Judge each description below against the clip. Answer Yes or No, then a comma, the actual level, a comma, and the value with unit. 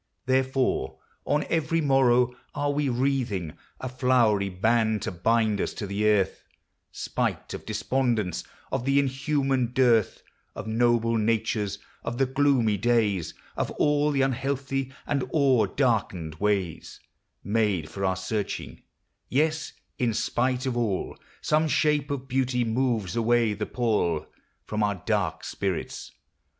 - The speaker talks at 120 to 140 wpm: Yes, slow, 135 wpm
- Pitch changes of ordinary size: Yes, average, 4.1 semitones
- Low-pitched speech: Yes, low, 120 Hz